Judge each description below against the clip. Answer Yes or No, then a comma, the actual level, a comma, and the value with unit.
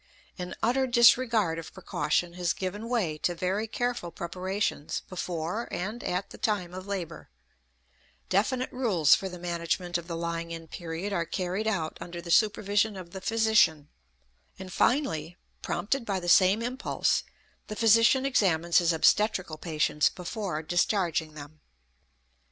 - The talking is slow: No, average, 145 wpm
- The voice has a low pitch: No, medium, 185 Hz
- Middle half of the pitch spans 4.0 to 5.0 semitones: Yes, average, 4.4 semitones